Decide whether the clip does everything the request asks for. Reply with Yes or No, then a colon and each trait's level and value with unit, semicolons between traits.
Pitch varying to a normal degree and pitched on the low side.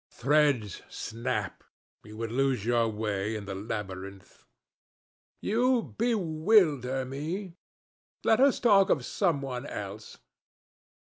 No: wide, 9.0 semitones; low, 130 Hz